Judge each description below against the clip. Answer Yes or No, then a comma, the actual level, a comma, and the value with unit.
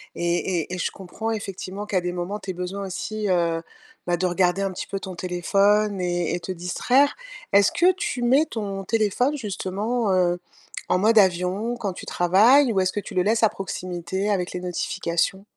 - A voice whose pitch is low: No, high, 195 Hz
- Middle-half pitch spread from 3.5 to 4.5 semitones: No, average, 3.0 semitones